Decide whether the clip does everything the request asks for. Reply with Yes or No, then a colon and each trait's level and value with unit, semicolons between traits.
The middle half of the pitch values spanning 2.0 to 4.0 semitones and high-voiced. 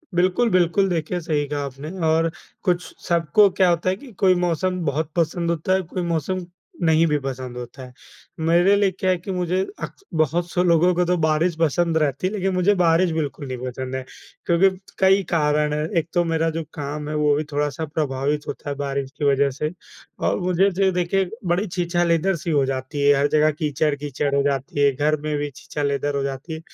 No: average, 3.6 semitones; medium, 160 Hz